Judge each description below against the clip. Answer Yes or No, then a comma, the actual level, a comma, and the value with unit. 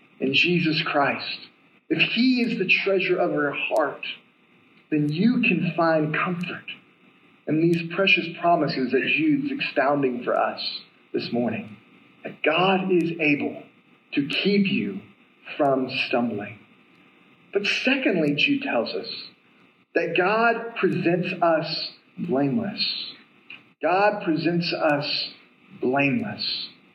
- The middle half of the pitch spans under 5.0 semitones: No, wide, 5.4 semitones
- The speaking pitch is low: No, medium, 170 Hz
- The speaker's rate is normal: No, slow, 110 wpm